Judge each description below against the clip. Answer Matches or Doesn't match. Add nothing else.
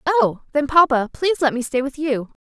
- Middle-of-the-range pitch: Doesn't match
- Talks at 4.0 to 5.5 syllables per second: Matches